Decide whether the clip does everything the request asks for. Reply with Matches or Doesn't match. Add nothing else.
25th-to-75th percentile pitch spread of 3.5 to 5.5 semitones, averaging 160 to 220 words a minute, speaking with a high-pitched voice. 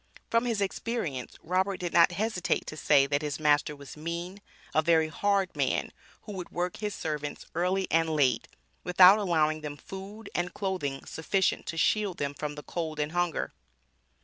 Doesn't match